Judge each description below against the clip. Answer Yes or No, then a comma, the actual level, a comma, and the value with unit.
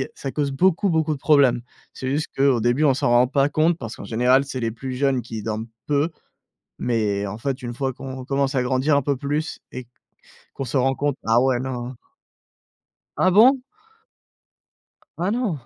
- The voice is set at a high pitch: No, low, 135 Hz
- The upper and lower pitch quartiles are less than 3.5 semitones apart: Yes, average, 3.1 semitones